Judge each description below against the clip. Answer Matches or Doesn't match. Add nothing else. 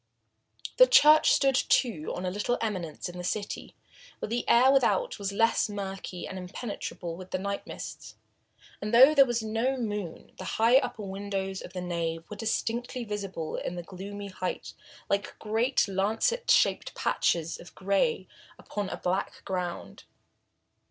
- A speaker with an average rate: Matches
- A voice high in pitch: Matches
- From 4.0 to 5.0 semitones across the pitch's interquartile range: Matches